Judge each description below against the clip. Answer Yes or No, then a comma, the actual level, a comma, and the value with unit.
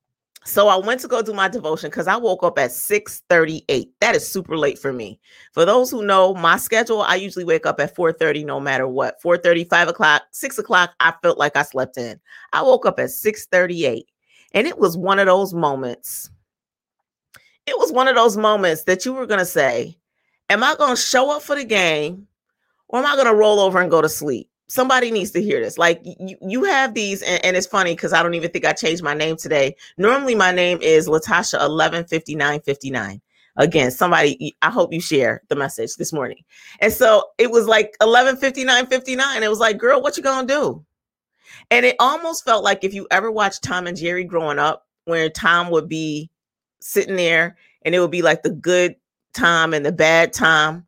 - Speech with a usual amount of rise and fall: No, wide, 6.1 semitones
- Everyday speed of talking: No, fast, 210 wpm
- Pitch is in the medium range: Yes, medium, 180 Hz